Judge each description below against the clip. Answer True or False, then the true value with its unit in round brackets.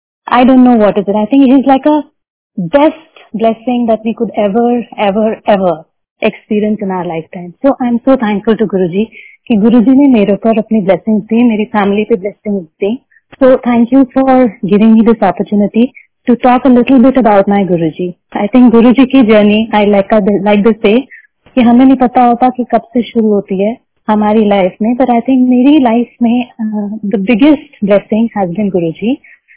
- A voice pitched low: False (225 Hz)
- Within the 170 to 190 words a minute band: True (180 wpm)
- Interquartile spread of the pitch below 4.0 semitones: True (3.4 semitones)